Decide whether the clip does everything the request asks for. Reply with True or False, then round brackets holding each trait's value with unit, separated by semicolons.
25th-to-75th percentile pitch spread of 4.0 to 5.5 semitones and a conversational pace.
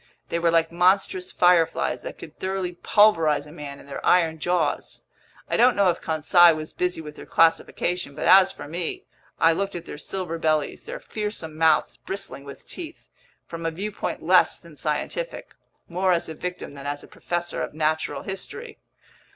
False (3.1 semitones; 175 wpm)